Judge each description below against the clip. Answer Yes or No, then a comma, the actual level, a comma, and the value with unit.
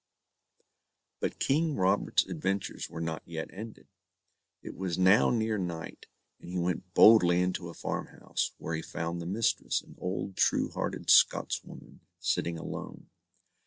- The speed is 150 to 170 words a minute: No, average, 140 wpm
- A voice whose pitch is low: Yes, very low, 90 Hz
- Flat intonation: No, average, 3.0 semitones